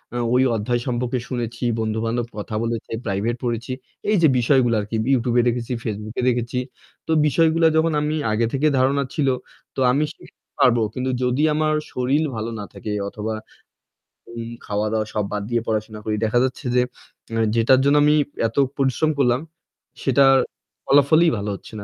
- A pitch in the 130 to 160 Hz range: No, low, 120 Hz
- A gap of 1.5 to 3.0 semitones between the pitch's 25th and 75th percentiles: No, average, 3.5 semitones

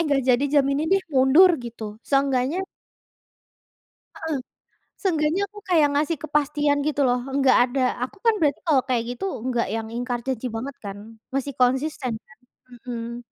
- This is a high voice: Yes, very high, 275 Hz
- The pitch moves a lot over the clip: No, average, 3.7 semitones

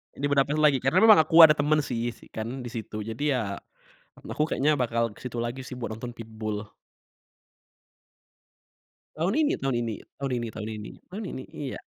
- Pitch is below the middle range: Yes, low, 130 Hz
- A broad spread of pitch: No, average, 4.4 semitones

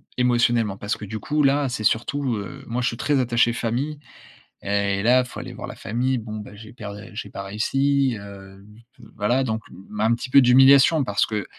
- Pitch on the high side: No, low, 115 Hz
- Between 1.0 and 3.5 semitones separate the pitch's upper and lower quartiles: No, average, 4.0 semitones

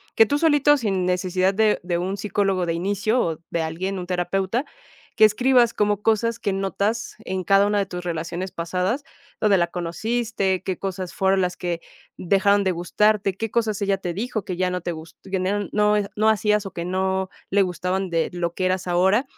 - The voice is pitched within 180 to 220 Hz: Yes, high, 190 Hz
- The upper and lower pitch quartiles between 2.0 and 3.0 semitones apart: Yes, average, 2.7 semitones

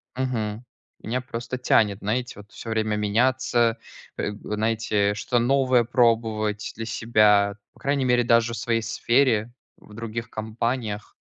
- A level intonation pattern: Yes, narrow, 2.3 semitones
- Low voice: Yes, low, 115 Hz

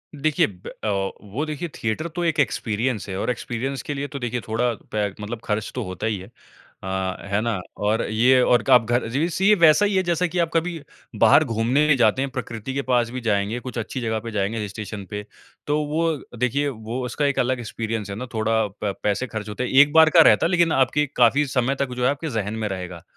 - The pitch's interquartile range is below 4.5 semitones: No, average, 5.0 semitones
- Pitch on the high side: No, low, 120 Hz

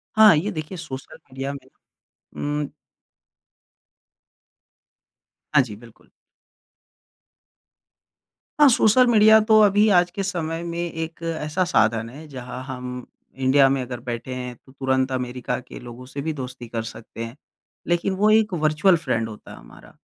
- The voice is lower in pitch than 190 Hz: Yes, medium, 140 Hz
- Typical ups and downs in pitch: No, wide, 5.7 semitones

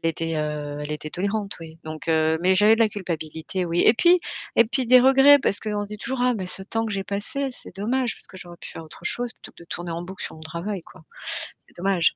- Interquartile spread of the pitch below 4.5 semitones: No, wide, 5.4 semitones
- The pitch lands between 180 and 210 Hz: Yes, high, 190 Hz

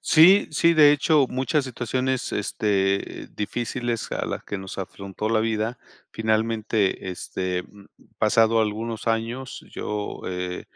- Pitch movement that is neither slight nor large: Yes, average, 3.8 semitones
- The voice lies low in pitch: Yes, low, 110 Hz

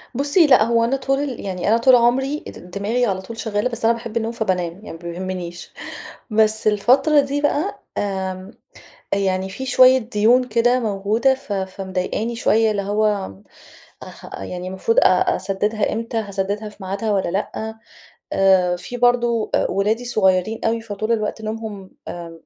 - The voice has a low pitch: No, high, 215 Hz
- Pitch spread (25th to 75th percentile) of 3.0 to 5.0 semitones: Yes, average, 3.5 semitones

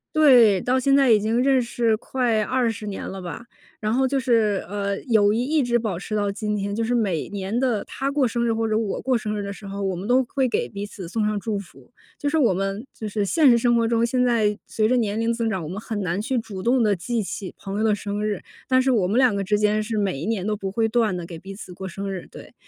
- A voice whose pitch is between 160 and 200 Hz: No, high, 215 Hz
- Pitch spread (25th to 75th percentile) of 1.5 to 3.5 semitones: Yes, average, 3.2 semitones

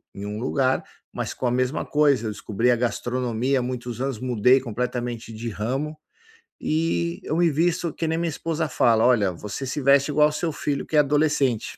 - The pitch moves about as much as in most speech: Yes, average, 4.2 semitones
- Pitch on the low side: Yes, low, 130 Hz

